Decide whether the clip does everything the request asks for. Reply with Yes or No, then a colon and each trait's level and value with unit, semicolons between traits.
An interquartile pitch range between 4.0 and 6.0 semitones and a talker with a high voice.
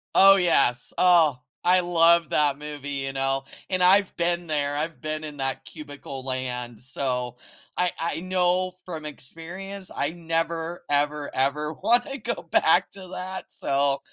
No: average, 4.3 semitones; medium, 155 Hz